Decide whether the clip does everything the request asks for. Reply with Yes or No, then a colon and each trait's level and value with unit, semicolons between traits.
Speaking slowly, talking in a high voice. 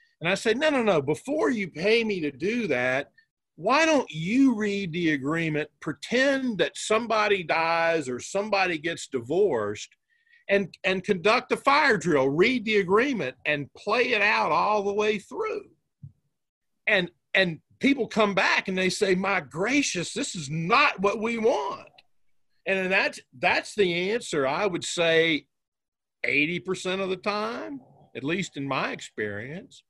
No: average, 155 wpm; high, 200 Hz